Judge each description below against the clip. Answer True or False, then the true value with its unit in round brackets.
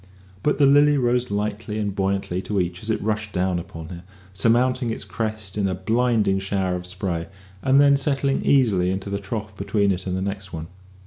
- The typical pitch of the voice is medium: False (100 Hz)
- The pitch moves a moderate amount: True (4.1 semitones)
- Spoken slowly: False (200 wpm)